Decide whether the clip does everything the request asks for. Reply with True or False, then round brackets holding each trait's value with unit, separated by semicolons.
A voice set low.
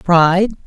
False (180 Hz)